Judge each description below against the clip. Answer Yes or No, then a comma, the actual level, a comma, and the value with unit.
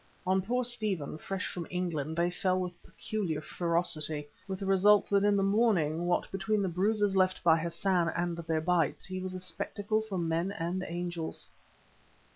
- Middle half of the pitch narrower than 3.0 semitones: Yes, narrow, 2.6 semitones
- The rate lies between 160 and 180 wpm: Yes, average, 175 wpm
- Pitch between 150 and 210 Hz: Yes, medium, 185 Hz